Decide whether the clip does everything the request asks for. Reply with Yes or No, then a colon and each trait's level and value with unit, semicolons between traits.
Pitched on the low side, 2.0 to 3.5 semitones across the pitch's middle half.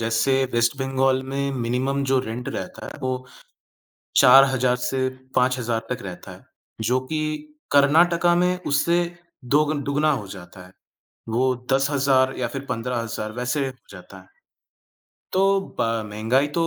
Yes: low, 130 Hz; average, 3.1 semitones